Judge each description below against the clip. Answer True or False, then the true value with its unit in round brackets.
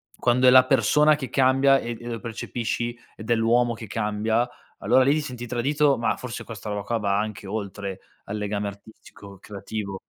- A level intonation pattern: False (3.4 semitones)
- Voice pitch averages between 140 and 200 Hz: False (115 Hz)